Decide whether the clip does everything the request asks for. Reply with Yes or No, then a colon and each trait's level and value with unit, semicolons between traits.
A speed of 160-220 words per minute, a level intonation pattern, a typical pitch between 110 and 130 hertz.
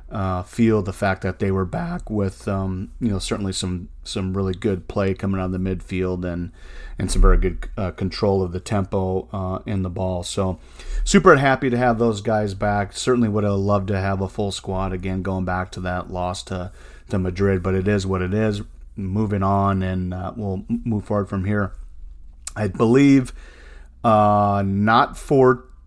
No: average, 195 wpm; narrow, 2.0 semitones; very low, 95 Hz